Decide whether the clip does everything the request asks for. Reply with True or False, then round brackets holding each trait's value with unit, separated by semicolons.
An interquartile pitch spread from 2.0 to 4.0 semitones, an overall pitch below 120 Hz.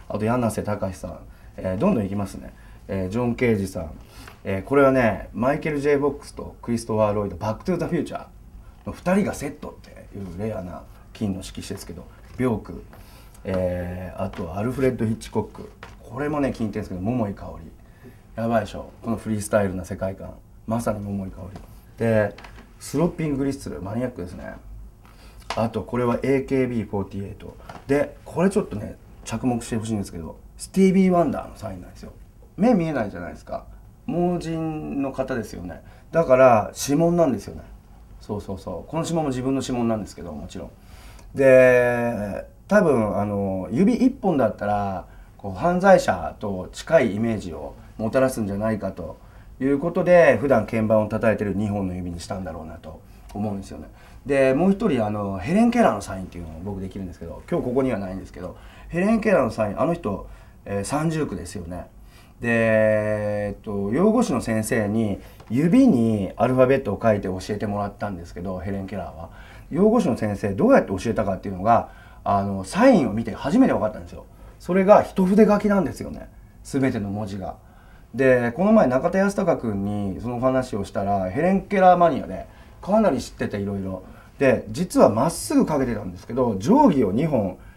False (5.2 semitones; 110 Hz)